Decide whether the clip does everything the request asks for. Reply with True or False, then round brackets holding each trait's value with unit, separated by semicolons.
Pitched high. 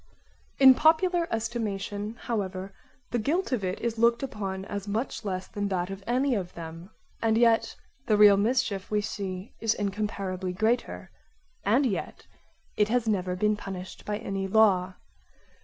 True (210 Hz)